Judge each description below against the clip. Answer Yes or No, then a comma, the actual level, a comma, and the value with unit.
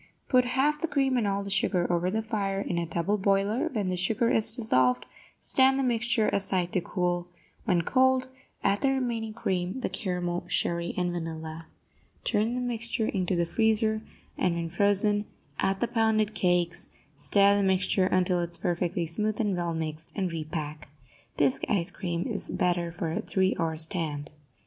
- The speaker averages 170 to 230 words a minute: Yes, average, 180 wpm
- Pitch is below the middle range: No, high, 190 Hz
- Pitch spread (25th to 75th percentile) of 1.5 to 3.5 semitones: No, average, 4.2 semitones